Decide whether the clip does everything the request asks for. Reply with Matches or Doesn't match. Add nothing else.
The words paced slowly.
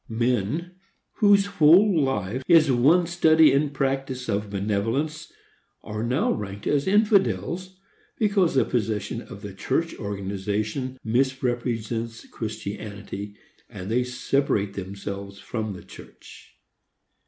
Matches